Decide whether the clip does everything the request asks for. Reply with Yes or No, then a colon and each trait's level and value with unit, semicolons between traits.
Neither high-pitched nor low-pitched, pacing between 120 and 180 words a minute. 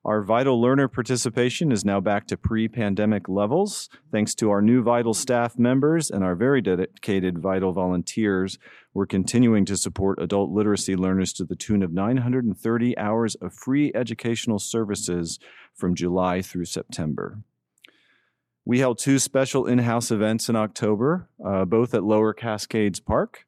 No: low, 110 Hz; average, 155 wpm